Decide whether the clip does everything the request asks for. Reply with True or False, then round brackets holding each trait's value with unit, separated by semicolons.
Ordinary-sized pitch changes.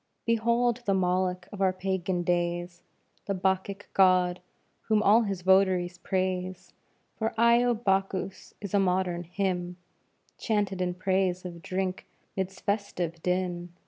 False (1.7 semitones)